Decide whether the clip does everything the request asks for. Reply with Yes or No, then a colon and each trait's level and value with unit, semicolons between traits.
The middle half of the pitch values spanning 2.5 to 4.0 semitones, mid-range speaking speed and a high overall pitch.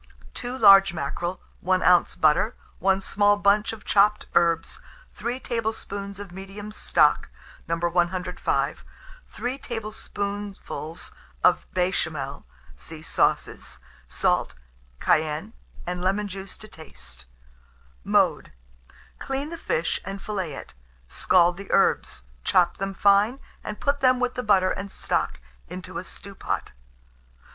No: average, 3.3 semitones; slow, 120 wpm; high, 195 Hz